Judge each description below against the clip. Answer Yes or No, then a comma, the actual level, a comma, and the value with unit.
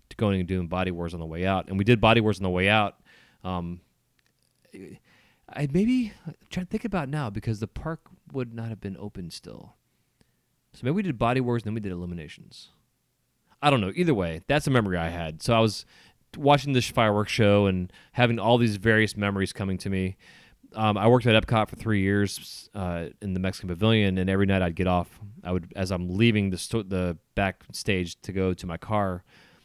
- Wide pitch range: No, average, 4.2 semitones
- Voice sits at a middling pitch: No, low, 100 Hz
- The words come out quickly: Yes, fast, 215 wpm